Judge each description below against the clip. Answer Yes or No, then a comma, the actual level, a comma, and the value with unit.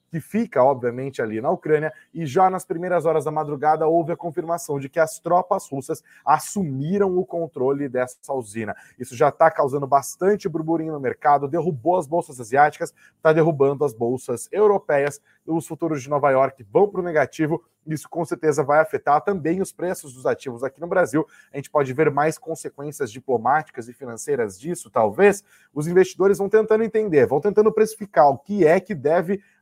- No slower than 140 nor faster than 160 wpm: No, average, 180 wpm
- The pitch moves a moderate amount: Yes, average, 4.3 semitones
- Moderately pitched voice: Yes, medium, 160 Hz